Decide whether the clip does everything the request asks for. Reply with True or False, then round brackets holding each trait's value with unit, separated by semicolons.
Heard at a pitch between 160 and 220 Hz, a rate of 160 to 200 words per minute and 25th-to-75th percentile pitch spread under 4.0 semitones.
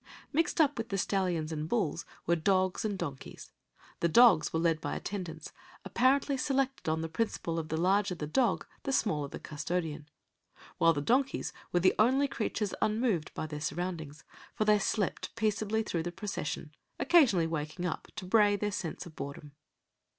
False (185 Hz; 170 wpm; 5.4 semitones)